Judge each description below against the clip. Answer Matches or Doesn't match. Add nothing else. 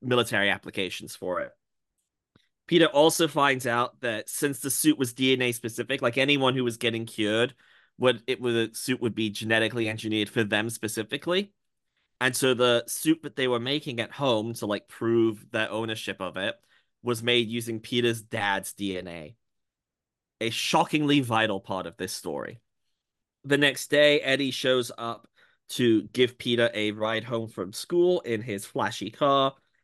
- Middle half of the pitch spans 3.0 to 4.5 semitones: Matches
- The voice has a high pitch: Doesn't match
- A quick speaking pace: Doesn't match